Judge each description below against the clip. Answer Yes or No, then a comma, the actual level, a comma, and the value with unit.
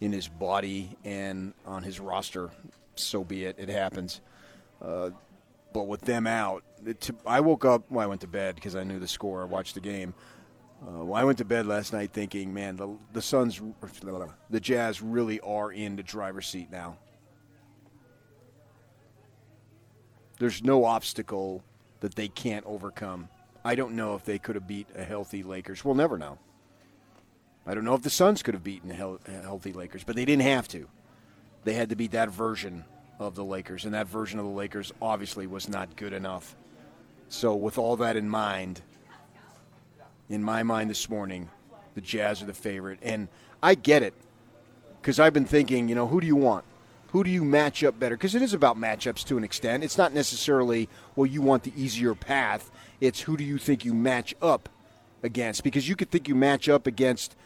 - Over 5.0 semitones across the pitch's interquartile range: No, average, 3.9 semitones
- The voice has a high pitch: No, low, 110 Hz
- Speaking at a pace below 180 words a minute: No, average, 195 wpm